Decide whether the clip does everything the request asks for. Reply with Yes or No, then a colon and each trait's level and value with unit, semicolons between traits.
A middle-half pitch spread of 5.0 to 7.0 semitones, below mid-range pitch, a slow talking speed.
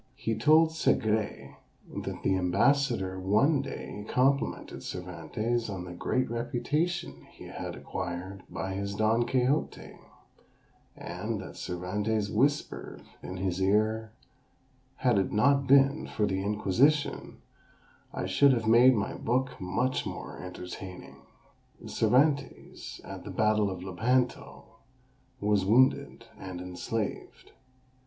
Yes: average, 5.3 semitones; low, 110 Hz; slow, 115 wpm